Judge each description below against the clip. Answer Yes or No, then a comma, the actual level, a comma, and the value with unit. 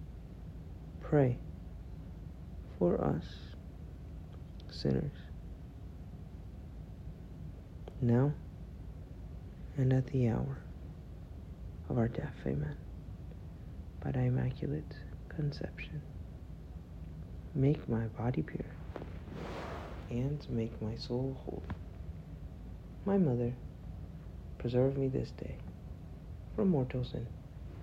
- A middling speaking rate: No, slow, 75 wpm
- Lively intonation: Yes, wide, 6.3 semitones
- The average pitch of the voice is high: No, very low, 85 Hz